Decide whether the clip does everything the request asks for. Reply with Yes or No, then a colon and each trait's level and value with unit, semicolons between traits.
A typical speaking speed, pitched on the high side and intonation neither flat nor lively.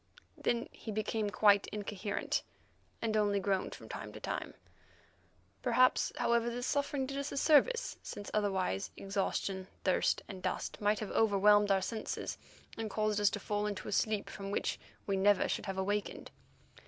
No: average, 165 wpm; high, 205 Hz; narrow, 1.9 semitones